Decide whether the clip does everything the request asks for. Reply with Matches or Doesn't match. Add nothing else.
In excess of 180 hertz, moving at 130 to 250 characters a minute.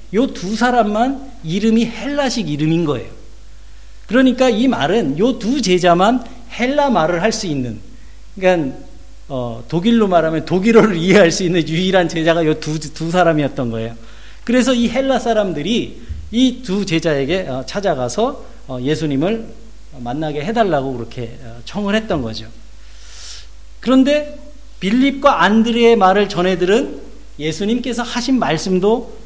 Doesn't match